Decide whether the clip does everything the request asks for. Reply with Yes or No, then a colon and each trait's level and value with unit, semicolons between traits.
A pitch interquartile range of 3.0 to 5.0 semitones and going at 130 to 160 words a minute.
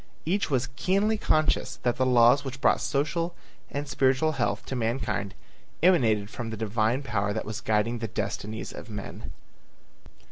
Yes: average, 4.7 semitones; average, 155 wpm